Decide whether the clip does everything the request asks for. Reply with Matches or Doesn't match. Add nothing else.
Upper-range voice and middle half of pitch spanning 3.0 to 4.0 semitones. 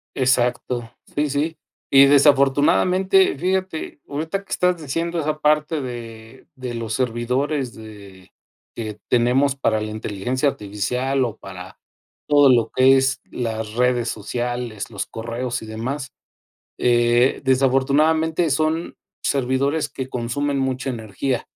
Doesn't match